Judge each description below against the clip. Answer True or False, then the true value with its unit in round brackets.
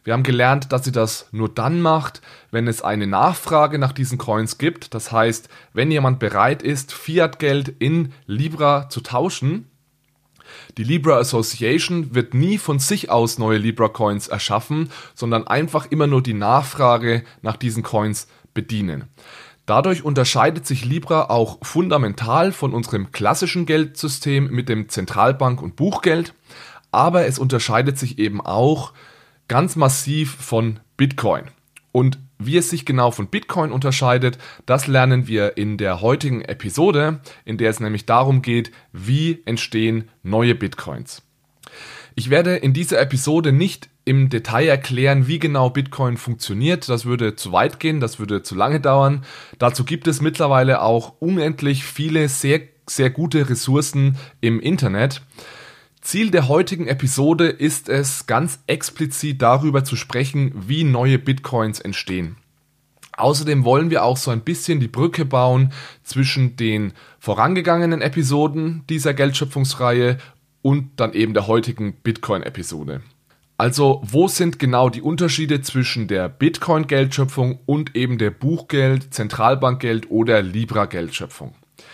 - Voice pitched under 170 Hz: True (135 Hz)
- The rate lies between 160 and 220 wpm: False (140 wpm)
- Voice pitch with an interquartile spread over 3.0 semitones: True (4.5 semitones)